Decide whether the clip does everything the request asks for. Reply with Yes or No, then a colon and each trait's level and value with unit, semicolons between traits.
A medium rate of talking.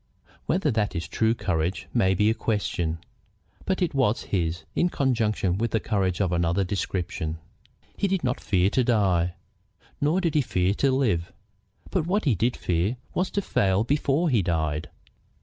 Yes: average, 165 wpm